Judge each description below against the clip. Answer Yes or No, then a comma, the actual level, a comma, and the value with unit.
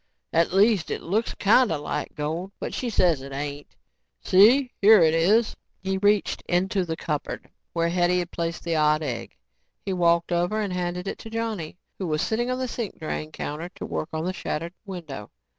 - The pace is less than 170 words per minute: No, average, 190 wpm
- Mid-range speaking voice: Yes, medium, 175 Hz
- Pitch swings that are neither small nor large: Yes, average, 4.2 semitones